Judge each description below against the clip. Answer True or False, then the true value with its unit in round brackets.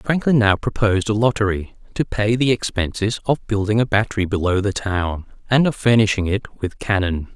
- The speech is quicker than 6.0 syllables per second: False (5.3 syllables/s)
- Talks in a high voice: False (105 Hz)